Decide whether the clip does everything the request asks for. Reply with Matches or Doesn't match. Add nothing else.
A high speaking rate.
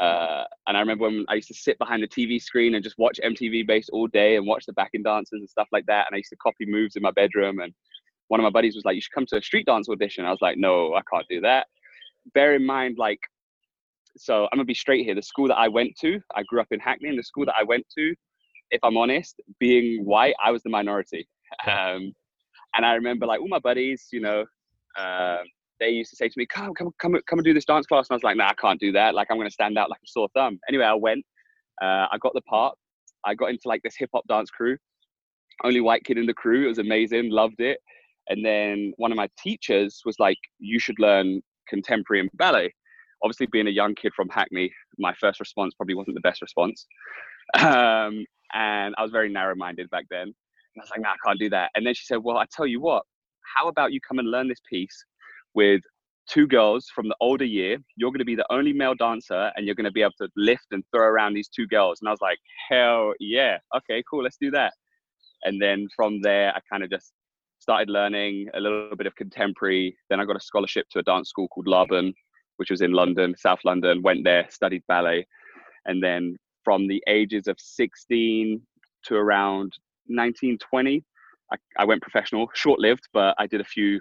Matches